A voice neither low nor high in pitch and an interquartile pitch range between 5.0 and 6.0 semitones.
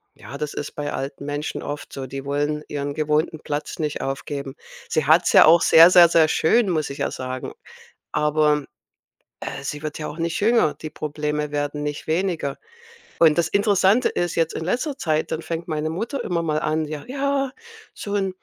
No: medium, 155 Hz; narrow, 2.6 semitones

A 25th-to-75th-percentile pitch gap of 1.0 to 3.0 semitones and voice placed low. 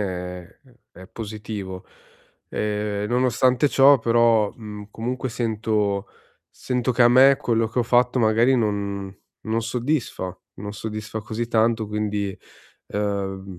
Yes: average, 2.7 semitones; low, 110 Hz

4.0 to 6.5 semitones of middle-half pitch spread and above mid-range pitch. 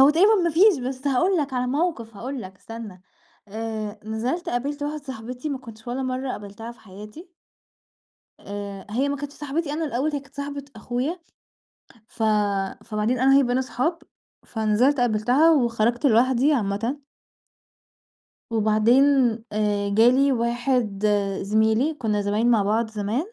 Yes: average, 4.4 semitones; high, 245 Hz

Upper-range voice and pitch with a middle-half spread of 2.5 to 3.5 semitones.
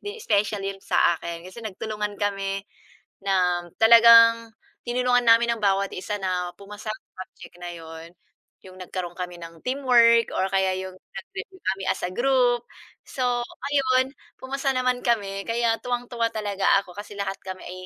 No: high, 205 Hz; average, 4.1 semitones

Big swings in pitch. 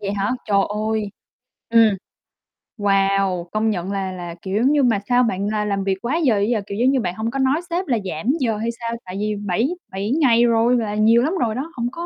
No: average, 3.6 semitones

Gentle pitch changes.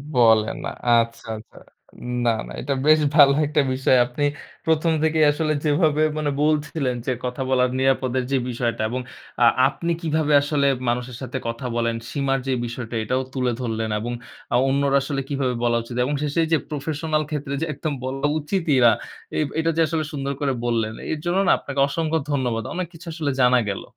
No: average, 3.7 semitones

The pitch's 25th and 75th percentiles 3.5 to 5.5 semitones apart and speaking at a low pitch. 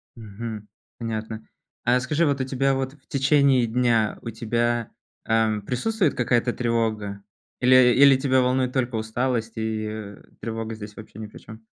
No: average, 2.7 semitones; low, 120 Hz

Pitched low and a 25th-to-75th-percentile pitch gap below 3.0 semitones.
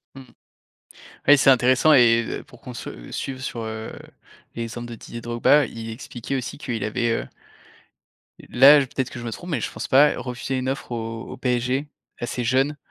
Yes: low, 125 Hz; narrow, 2.5 semitones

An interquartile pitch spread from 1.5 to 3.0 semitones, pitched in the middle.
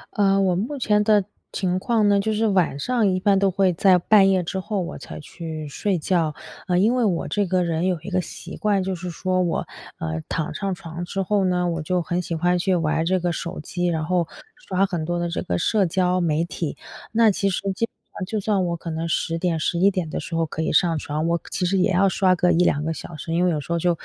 Yes: average, 2.7 semitones; medium, 180 Hz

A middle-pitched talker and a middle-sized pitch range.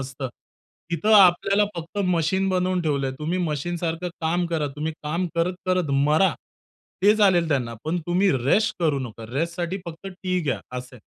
Yes: medium, 170 Hz; average, 3.3 semitones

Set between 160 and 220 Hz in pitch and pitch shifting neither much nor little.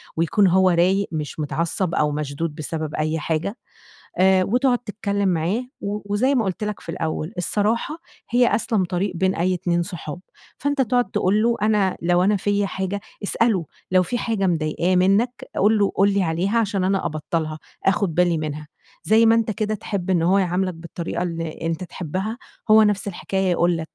Yes: high, 190 Hz; average, 3.7 semitones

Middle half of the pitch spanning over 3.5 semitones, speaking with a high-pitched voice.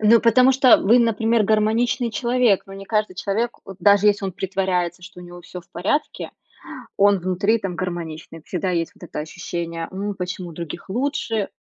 Yes: average, 3.9 semitones; high, 195 Hz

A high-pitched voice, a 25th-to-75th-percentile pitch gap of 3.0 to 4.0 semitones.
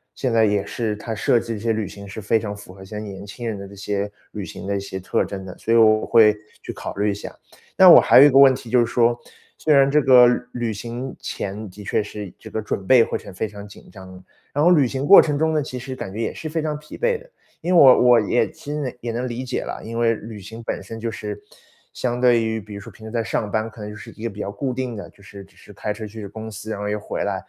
No: low, 110 Hz; average, 3.3 semitones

